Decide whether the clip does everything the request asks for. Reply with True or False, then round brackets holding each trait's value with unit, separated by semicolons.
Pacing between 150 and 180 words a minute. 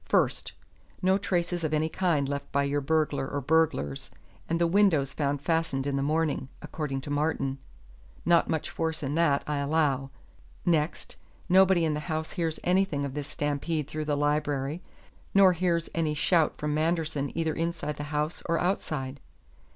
True (165 wpm)